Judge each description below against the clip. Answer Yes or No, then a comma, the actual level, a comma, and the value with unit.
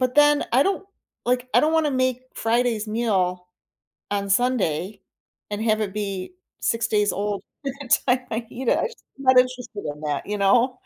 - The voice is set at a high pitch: Yes, high, 230 Hz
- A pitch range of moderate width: Yes, average, 4.0 semitones